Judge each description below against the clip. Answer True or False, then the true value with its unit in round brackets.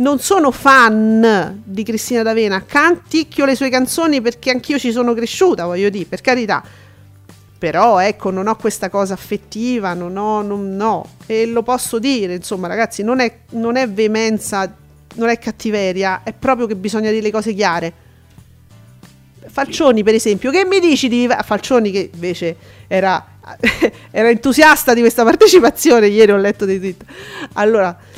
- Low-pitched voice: False (220 Hz)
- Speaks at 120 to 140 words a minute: False (160 wpm)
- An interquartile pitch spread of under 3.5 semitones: False (4.4 semitones)